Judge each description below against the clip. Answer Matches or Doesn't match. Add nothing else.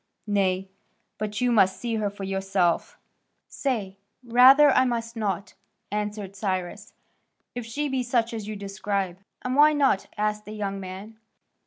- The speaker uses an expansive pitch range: Doesn't match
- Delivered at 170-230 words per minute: Doesn't match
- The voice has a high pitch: Matches